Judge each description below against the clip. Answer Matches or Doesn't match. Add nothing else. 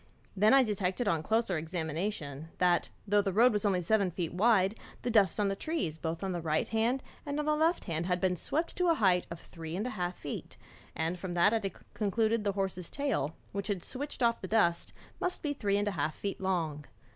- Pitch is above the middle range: Matches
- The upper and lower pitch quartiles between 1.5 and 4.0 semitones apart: Doesn't match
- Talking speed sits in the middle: Doesn't match